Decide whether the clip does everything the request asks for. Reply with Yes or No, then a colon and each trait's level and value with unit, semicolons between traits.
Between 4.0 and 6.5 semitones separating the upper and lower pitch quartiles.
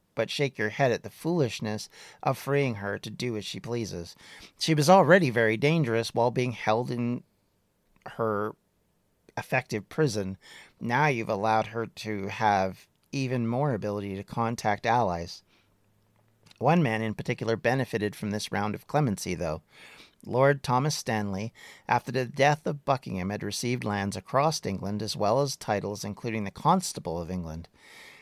Yes: average, 4.4 semitones